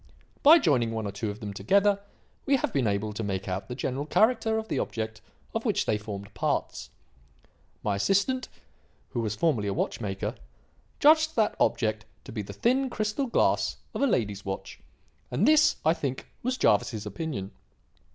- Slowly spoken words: No, average, 180 wpm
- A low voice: Yes, low, 120 Hz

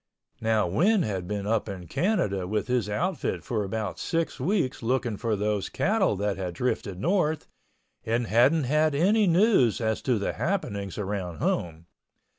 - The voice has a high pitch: No, low, 115 Hz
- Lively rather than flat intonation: Yes, wide, 7.8 semitones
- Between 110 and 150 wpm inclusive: No, average, 160 wpm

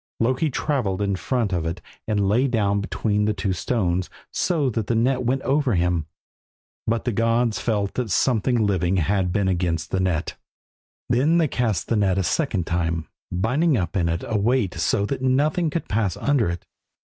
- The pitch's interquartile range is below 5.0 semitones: No, wide, 5.4 semitones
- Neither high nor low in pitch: No, low, 105 Hz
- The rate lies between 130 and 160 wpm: No, average, 185 wpm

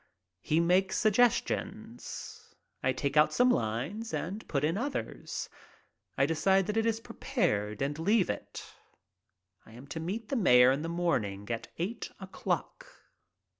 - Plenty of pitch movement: Yes, wide, 8.0 semitones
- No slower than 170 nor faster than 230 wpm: No, average, 145 wpm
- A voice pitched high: No, medium, 170 Hz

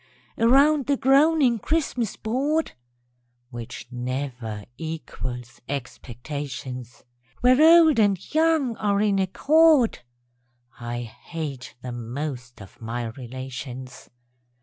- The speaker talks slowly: Yes, slow, 100 wpm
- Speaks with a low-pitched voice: No, medium, 155 Hz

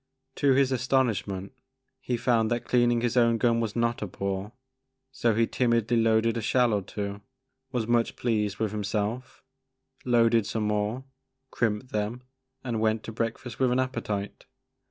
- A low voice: Yes, low, 115 Hz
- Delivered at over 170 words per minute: No, average, 155 wpm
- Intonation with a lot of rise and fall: No, narrow, 2.4 semitones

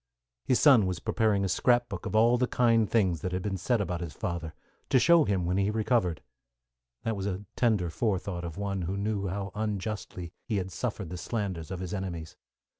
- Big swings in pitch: No, average, 3.4 semitones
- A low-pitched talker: Yes, low, 100 Hz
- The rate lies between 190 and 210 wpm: Yes, fast, 205 wpm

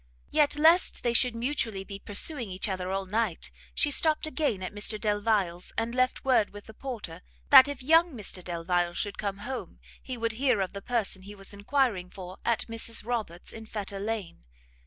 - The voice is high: Yes, high, 215 Hz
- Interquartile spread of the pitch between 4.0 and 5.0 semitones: Yes, average, 4.6 semitones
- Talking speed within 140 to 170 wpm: No, average, 190 wpm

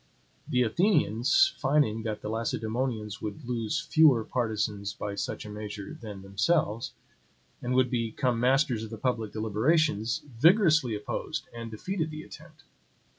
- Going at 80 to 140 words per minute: Yes, slow, 135 wpm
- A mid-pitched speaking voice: No, low, 115 Hz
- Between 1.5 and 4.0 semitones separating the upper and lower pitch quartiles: No, average, 5.3 semitones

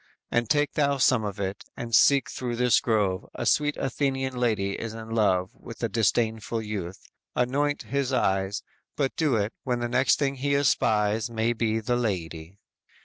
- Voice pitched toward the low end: Yes, low, 115 Hz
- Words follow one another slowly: No, average, 175 wpm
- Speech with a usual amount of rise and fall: Yes, average, 3.9 semitones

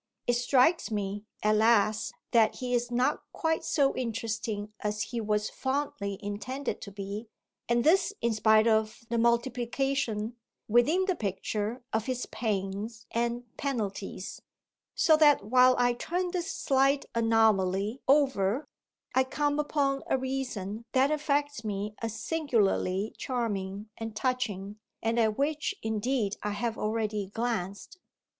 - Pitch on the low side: No, high, 230 Hz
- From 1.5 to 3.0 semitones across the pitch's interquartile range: No, average, 4.0 semitones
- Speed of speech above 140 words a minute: No, slow, 135 wpm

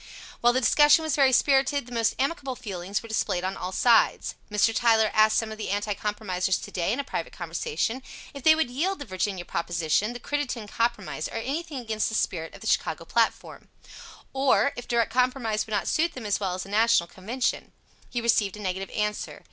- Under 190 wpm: No, fast, 205 wpm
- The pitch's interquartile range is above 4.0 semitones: Yes, average, 4.6 semitones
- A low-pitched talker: No, high, 225 Hz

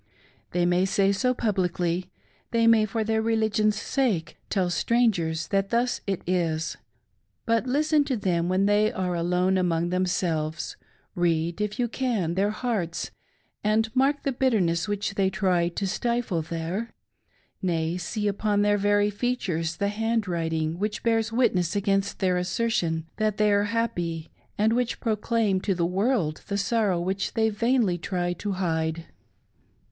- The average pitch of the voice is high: Yes, high, 200 Hz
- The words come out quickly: No, average, 150 wpm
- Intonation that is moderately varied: Yes, average, 4.1 semitones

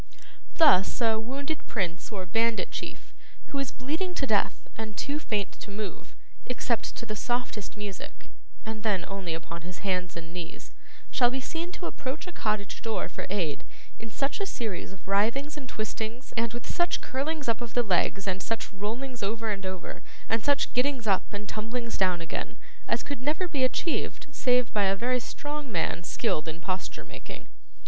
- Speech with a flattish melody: No, average, 4.8 semitones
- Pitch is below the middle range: No, high, 225 Hz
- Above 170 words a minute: Yes, average, 185 wpm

